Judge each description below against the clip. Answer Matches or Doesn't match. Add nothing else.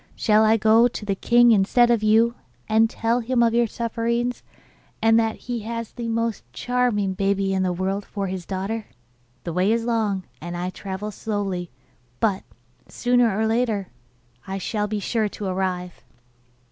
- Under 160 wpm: Doesn't match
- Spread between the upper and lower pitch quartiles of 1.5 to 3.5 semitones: Matches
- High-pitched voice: Matches